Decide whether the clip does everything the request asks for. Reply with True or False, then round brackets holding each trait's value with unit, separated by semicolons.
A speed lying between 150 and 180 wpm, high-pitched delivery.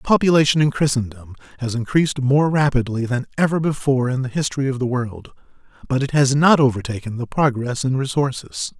False (170 wpm; 135 Hz)